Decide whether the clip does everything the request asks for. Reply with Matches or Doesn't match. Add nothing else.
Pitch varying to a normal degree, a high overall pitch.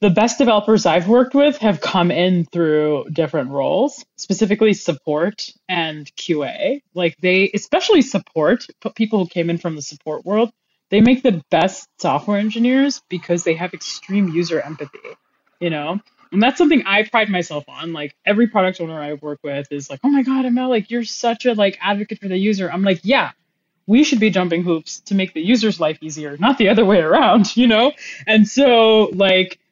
Doesn't match